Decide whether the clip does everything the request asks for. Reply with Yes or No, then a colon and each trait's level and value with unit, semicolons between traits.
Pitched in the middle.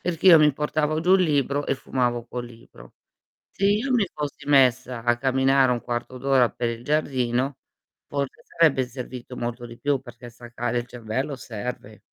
No: low, 130 Hz